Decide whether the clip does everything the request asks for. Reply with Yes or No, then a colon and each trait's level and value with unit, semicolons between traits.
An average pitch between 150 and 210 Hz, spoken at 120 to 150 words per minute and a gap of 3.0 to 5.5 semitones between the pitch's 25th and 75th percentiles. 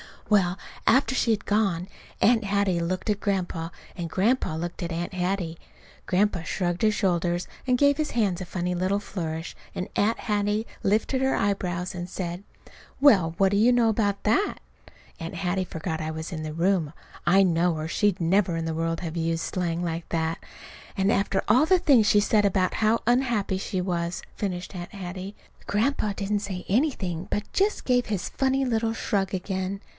No: high, 190 Hz; average, 180 wpm; average, 3.4 semitones